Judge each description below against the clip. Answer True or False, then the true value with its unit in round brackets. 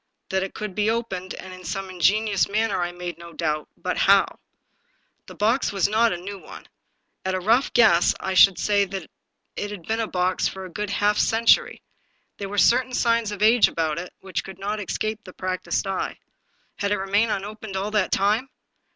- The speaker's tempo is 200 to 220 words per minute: True (205 wpm)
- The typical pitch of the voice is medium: False (200 Hz)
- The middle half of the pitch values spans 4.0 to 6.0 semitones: False (2.6 semitones)